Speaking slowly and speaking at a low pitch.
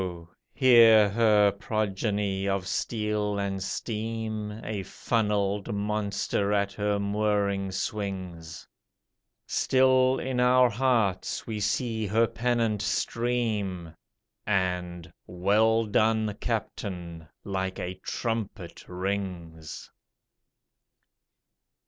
Yes: slow, 85 wpm; low, 105 Hz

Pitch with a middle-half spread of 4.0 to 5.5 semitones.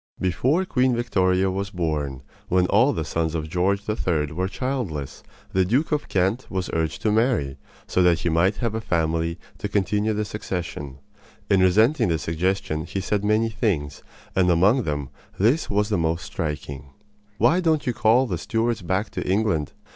Yes: average, 5.1 semitones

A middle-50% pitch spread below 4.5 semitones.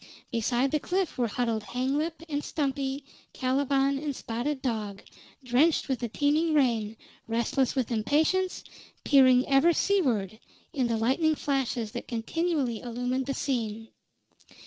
Yes: average, 3.8 semitones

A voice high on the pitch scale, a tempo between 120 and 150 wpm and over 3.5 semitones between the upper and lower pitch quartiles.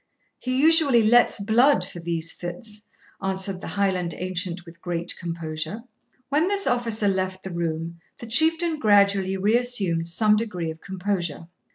Yes: high, 195 Hz; average, 145 wpm; average, 5.2 semitones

